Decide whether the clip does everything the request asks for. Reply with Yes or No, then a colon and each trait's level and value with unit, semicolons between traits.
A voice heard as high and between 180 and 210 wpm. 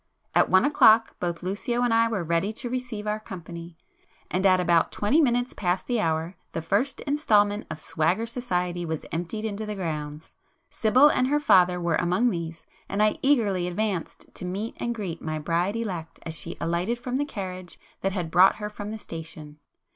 Yes: high, 195 Hz; average, 185 wpm